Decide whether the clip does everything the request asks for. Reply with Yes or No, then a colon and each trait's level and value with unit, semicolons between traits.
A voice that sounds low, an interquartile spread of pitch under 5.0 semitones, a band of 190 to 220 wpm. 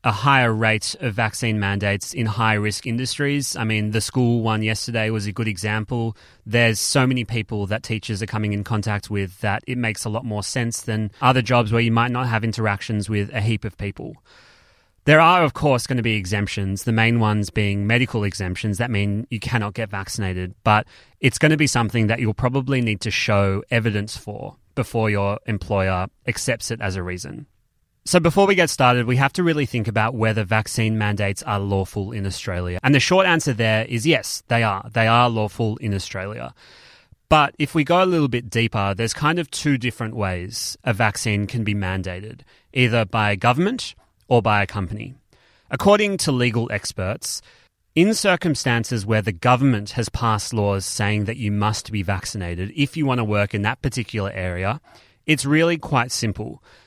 Yes: low, 110 Hz; average, 3.2 semitones; average, 195 wpm